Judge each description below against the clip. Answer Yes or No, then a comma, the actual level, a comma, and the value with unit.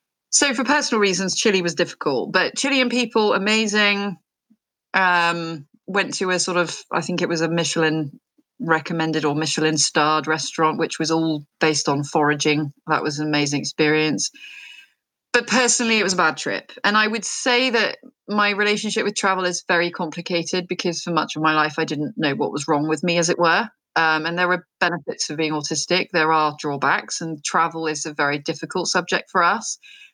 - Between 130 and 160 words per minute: No, average, 190 wpm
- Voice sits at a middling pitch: Yes, medium, 170 Hz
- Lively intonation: No, average, 4.6 semitones